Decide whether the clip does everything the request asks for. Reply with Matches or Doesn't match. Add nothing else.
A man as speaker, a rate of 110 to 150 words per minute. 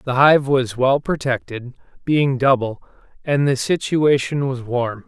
Matches